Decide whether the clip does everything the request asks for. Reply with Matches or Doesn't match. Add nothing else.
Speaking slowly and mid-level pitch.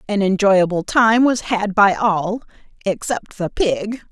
Doesn't match